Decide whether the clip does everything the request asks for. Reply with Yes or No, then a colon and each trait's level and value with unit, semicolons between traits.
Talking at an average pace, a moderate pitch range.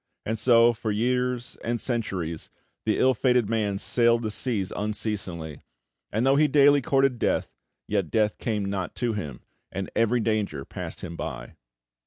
Yes: average, 160 wpm; average, 3.6 semitones